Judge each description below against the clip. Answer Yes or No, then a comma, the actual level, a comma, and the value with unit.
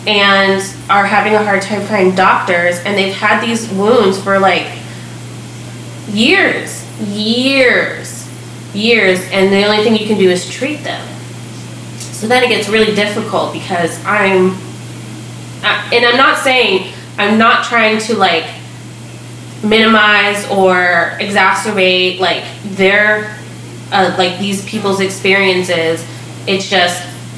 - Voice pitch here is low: No, high, 195 Hz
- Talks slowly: Yes, slow, 125 wpm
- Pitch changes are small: Yes, narrow, 2.2 semitones